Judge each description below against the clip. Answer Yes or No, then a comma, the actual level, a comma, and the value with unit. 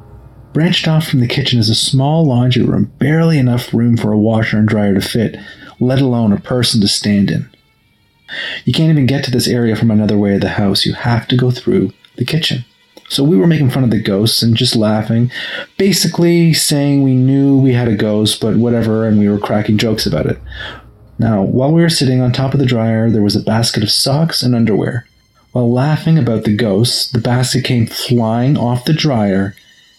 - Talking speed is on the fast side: Yes, fast, 210 wpm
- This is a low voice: Yes, low, 120 Hz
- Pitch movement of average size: Yes, average, 3.7 semitones